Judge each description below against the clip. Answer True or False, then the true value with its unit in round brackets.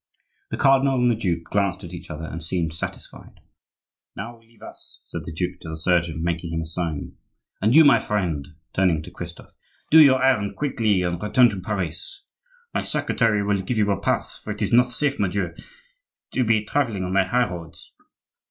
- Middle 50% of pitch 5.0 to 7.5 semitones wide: True (5.4 semitones)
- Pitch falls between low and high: False (100 Hz)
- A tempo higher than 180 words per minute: True (195 wpm)